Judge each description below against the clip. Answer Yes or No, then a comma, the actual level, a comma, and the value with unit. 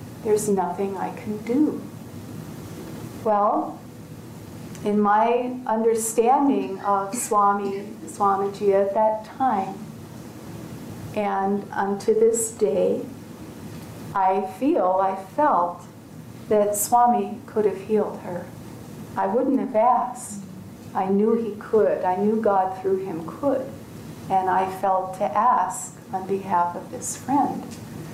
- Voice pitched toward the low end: No, high, 205 Hz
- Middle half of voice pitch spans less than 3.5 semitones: Yes, average, 2.9 semitones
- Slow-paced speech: Yes, slow, 115 wpm